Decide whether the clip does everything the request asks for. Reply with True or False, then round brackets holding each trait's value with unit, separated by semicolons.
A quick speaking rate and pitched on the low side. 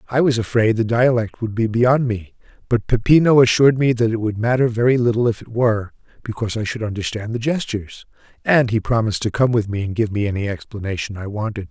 True (215 wpm; 115 Hz)